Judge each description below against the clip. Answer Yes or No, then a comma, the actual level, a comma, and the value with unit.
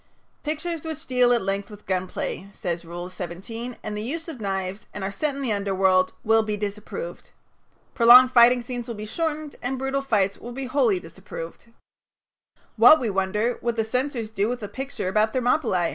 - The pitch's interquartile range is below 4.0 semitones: No, average, 4.6 semitones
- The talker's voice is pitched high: Yes, high, 225 Hz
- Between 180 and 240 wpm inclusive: Yes, average, 190 wpm